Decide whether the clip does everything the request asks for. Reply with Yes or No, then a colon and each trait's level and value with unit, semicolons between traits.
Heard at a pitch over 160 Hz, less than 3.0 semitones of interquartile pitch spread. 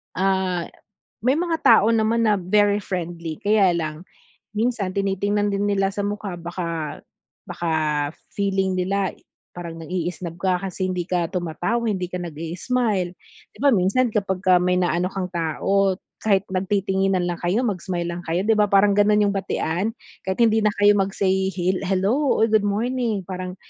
Yes: high, 190 Hz; narrow, 2.4 semitones